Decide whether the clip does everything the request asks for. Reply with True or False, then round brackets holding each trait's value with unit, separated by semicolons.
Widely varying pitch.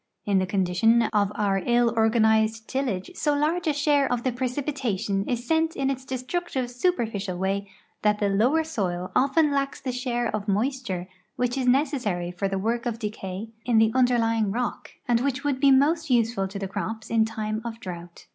False (4.5 semitones)